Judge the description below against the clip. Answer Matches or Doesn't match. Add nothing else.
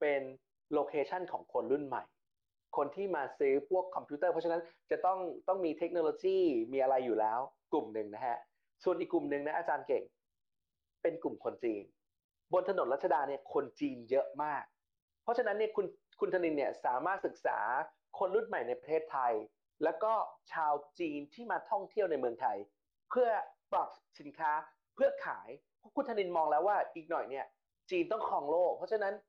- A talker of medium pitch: Matches